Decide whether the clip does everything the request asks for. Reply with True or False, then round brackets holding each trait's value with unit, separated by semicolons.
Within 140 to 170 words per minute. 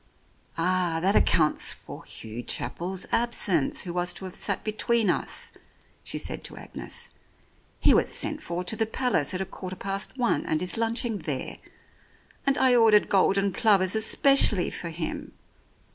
True (160 wpm)